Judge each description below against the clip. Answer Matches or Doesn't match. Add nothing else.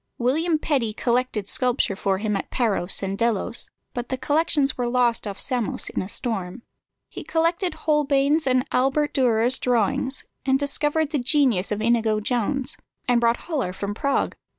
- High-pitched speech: Matches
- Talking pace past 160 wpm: Doesn't match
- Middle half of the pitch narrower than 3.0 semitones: Doesn't match